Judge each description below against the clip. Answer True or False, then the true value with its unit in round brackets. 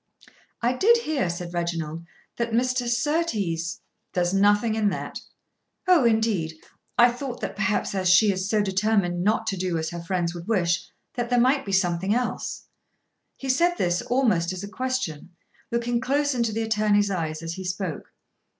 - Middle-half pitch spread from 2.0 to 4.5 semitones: False (5.4 semitones)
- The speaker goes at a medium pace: True (175 wpm)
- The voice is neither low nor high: False (205 Hz)